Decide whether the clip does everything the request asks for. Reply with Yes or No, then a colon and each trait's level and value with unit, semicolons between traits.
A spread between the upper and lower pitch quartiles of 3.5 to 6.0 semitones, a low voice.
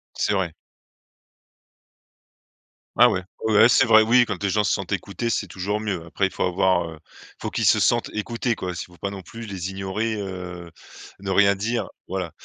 No: average, 2.9 semitones; low, 100 Hz